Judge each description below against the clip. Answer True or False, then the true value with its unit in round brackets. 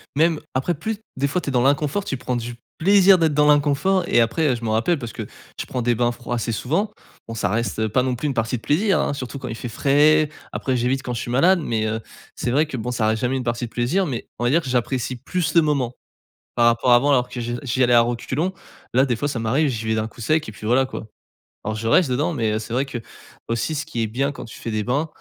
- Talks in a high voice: False (125 Hz)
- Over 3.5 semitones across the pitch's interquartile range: True (4.1 semitones)